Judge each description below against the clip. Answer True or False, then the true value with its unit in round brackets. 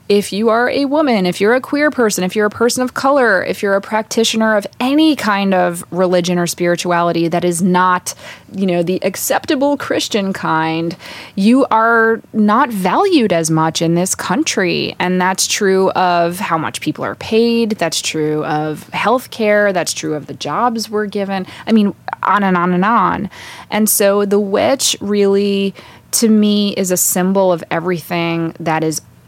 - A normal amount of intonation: True (4.1 semitones)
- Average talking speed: True (180 wpm)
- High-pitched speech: True (195 Hz)